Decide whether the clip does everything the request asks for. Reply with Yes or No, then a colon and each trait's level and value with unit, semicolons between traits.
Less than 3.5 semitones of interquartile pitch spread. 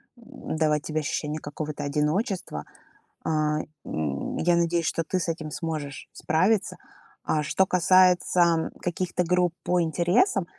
Yes: average, 2.9 semitones